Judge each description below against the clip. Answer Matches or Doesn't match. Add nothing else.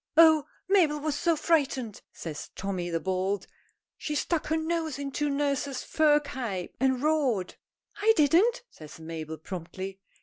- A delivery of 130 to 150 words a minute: Matches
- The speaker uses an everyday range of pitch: Doesn't match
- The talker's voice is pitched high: Matches